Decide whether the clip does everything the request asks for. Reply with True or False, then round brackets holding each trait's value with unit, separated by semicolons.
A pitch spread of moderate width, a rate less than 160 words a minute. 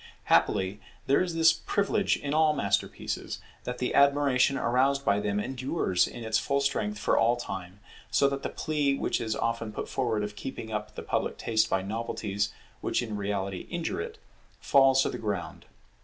False (5.0 semitones; 180 wpm)